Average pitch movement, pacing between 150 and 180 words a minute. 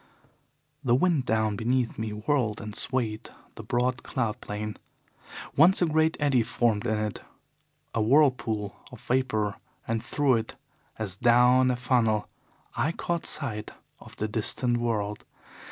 No: average, 3.2 semitones; average, 140 wpm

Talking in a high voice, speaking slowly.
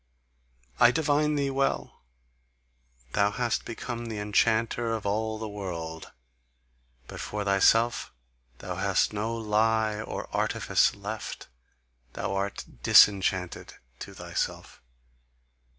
No: low, 110 Hz; slow, 105 wpm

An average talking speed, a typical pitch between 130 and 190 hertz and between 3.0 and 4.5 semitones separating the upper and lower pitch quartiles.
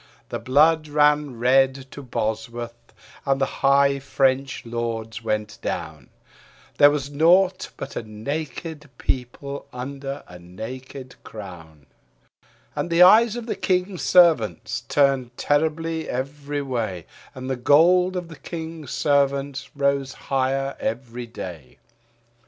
No: slow, 125 wpm; low, 135 Hz; average, 4.0 semitones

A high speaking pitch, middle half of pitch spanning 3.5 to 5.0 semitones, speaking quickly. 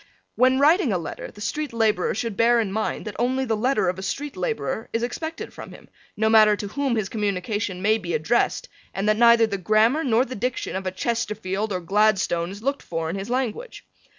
Yes: high, 220 Hz; average, 4.0 semitones; fast, 215 wpm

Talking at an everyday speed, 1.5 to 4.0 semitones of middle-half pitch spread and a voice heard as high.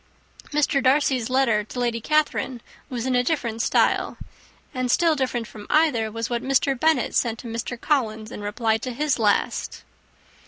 Yes: average, 165 wpm; average, 3.3 semitones; high, 245 Hz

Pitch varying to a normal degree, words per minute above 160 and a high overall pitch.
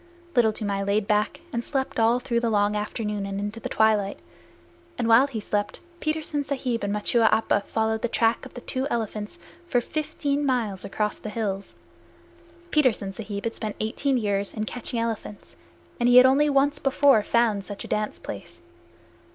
Yes: average, 3.3 semitones; average, 175 wpm; high, 225 Hz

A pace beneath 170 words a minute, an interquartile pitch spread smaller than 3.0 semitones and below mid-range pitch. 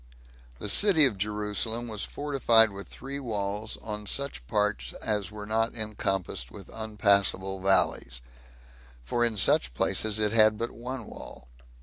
Yes: average, 140 wpm; narrow, 2.4 semitones; low, 105 Hz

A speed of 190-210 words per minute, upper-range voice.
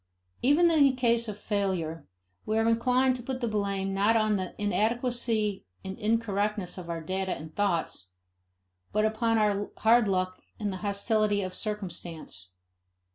No: average, 155 wpm; high, 210 Hz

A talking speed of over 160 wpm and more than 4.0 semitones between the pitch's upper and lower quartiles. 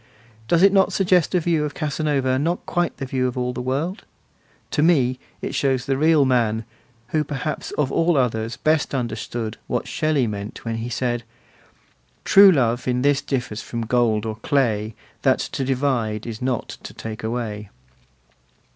Yes: average, 170 wpm; average, 4.5 semitones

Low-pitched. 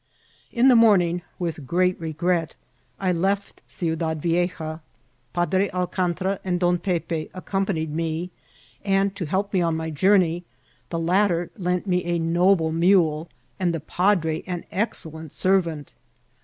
No: medium, 175 Hz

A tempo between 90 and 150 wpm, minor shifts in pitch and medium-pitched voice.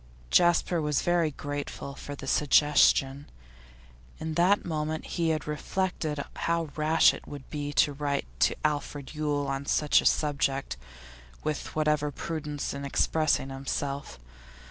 Yes: slow, 135 wpm; narrow, 1.8 semitones; medium, 150 Hz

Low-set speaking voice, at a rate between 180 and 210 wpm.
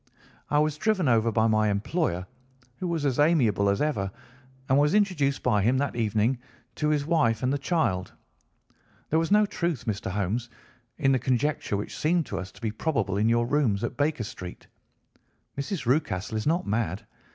Yes: low, 125 Hz; average, 185 wpm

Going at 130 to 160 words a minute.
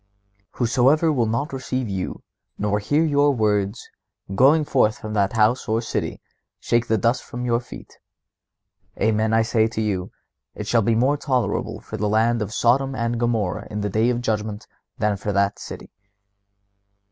No: average, 170 wpm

